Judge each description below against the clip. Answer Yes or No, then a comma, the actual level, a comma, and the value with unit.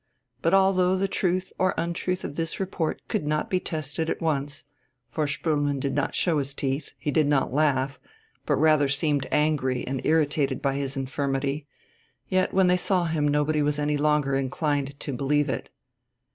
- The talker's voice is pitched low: No, medium, 150 Hz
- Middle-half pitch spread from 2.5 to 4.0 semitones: Yes, average, 2.8 semitones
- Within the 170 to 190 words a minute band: Yes, average, 175 wpm